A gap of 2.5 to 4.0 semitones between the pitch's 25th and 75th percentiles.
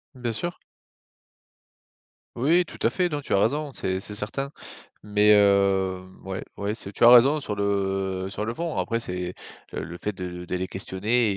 No: average, 4.4 semitones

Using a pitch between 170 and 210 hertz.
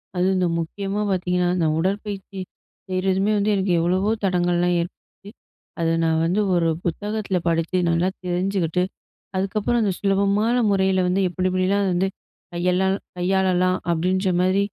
Yes: medium, 185 Hz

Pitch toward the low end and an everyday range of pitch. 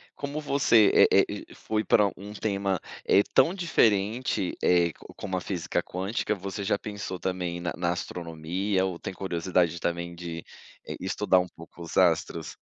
Yes: very low, 95 Hz; average, 3.1 semitones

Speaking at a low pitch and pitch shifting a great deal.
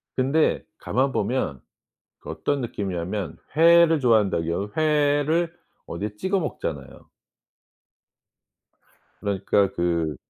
Yes: low, 110 Hz; wide, 8.5 semitones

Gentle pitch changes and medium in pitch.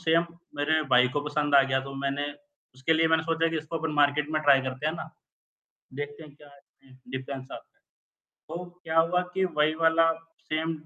Yes: narrow, 2.2 semitones; medium, 155 Hz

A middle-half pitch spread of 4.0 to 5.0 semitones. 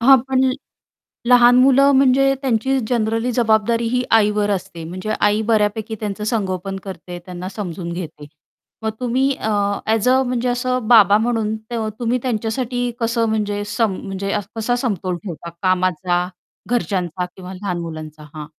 Yes: average, 4.7 semitones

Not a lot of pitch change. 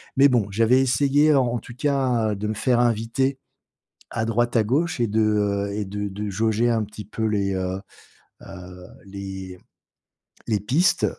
No: average, 3.5 semitones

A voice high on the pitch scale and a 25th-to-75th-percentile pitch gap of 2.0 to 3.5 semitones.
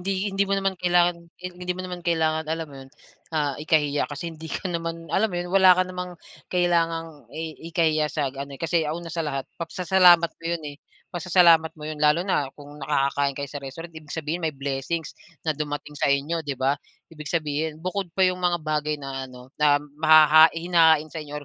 No: medium, 160 Hz; average, 2.9 semitones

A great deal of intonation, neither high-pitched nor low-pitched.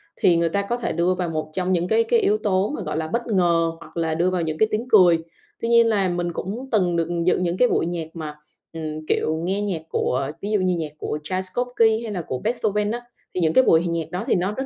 No: average, 4.3 semitones; medium, 180 Hz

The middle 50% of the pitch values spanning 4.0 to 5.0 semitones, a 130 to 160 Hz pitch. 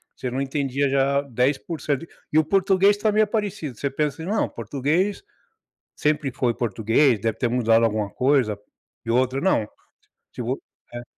Yes: average, 4.6 semitones; low, 135 Hz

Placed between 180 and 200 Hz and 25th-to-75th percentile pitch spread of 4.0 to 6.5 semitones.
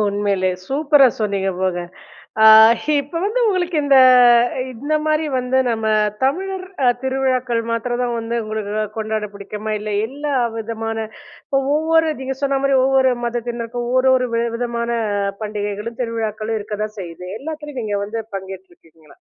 No: high, 235 Hz; average, 4.3 semitones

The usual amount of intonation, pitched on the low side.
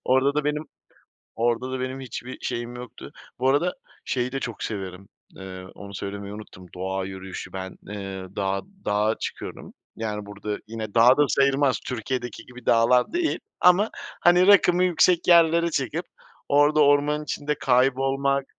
No: wide, 6.0 semitones; low, 125 Hz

